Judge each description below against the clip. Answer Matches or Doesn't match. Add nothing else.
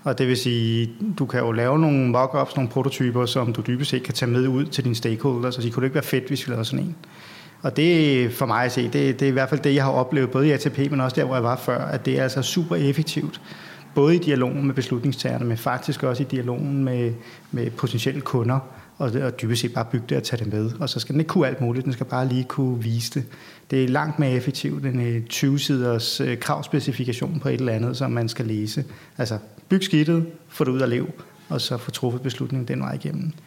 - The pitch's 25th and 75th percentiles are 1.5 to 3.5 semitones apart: Matches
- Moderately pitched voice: Doesn't match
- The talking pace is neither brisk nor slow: Doesn't match